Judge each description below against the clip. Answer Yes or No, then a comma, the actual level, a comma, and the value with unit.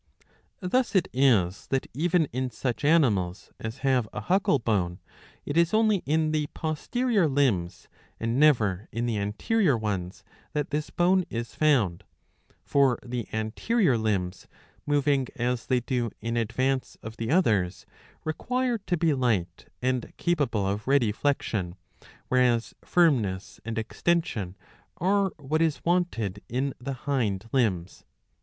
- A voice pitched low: Yes, low, 130 Hz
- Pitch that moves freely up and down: Yes, wide, 6.2 semitones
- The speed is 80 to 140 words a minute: Yes, slow, 135 wpm